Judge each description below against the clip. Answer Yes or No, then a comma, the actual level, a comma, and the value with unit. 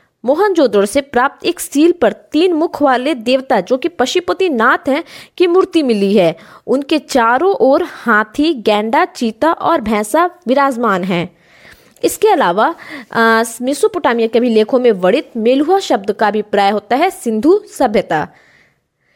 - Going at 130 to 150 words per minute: Yes, average, 140 wpm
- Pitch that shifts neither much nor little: No, wide, 6.7 semitones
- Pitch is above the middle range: Yes, very high, 260 Hz